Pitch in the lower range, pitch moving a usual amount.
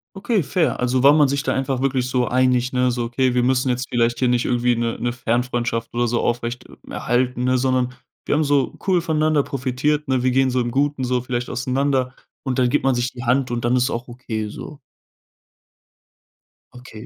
No: low, 125 Hz; narrow, 1.7 semitones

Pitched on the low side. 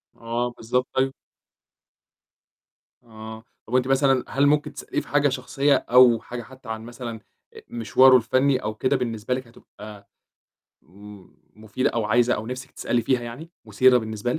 Yes: low, 120 Hz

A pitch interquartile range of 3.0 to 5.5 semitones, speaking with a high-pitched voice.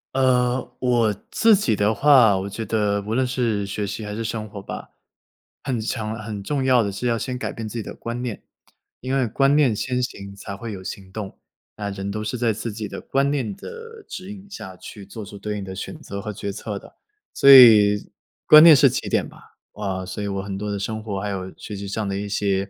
No: average, 3.8 semitones; low, 110 Hz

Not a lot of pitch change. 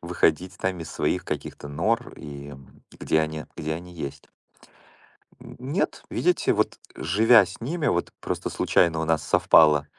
No: average, 4.5 semitones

